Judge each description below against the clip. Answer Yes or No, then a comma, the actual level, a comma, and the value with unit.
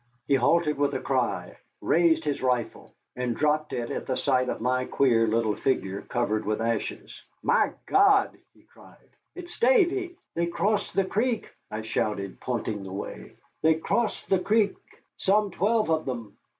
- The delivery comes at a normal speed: Yes, average, 165 wpm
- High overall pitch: No, medium, 145 Hz